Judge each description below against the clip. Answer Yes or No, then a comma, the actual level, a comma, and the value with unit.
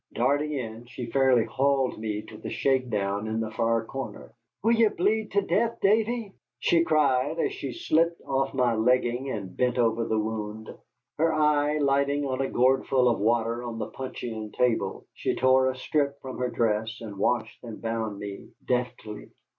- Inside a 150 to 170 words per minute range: No, average, 180 wpm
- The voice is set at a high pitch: No, low, 125 Hz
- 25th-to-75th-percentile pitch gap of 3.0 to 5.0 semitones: Yes, average, 4.1 semitones